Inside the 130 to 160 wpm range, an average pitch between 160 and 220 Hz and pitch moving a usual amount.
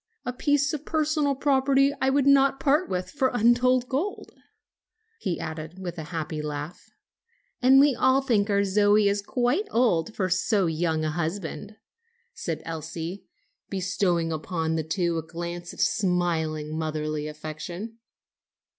No: average, 145 wpm; high, 190 Hz; wide, 8.0 semitones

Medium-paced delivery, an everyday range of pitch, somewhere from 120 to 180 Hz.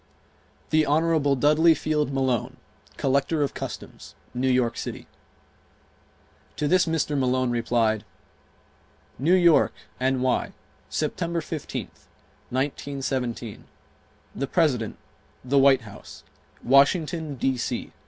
No: slow, 95 wpm; average, 3.4 semitones; medium, 140 Hz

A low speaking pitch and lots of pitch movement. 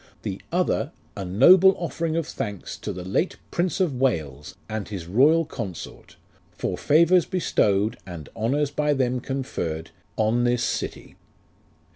Yes: low, 125 Hz; wide, 8.2 semitones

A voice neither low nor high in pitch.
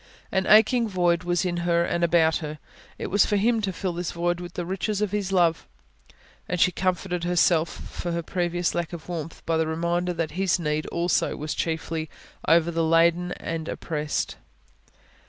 Yes: medium, 175 Hz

